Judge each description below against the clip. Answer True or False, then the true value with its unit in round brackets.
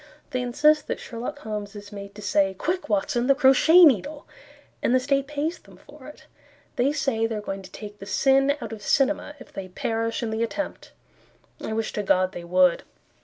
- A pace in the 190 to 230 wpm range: True (205 wpm)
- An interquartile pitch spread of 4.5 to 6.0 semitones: True (5.2 semitones)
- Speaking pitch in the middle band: False (230 Hz)